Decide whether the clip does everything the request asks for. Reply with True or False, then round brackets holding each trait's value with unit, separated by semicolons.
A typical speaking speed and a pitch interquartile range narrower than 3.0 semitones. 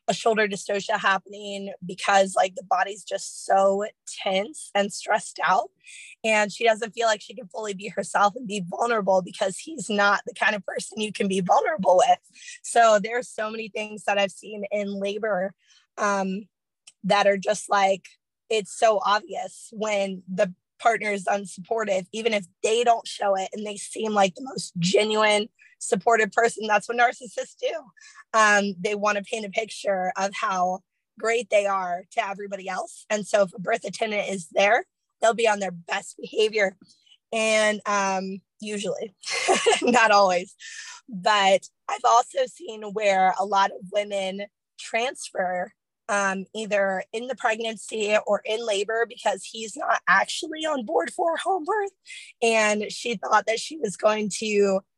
True (165 wpm; 2.5 semitones)